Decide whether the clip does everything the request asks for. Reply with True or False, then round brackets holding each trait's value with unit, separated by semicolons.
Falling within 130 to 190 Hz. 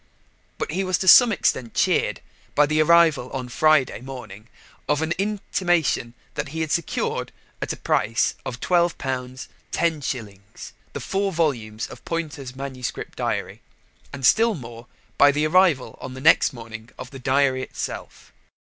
True (140 Hz)